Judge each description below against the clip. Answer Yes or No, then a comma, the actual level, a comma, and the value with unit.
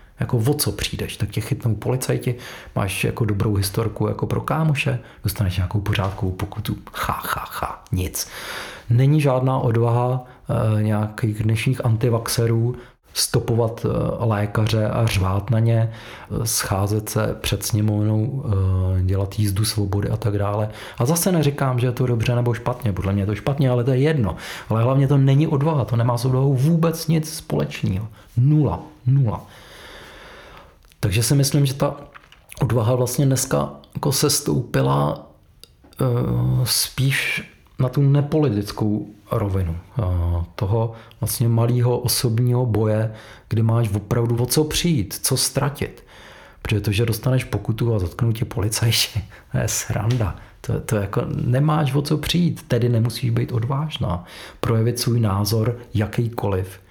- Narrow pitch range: No, average, 3.6 semitones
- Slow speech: No, average, 145 wpm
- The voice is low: Yes, low, 115 Hz